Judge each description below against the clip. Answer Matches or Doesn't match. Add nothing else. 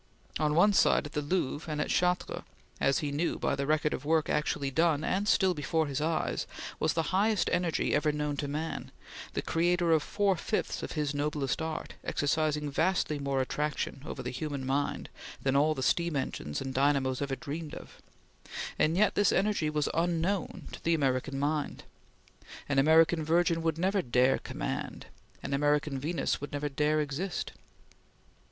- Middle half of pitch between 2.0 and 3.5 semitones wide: Matches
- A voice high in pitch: Doesn't match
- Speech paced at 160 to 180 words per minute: Matches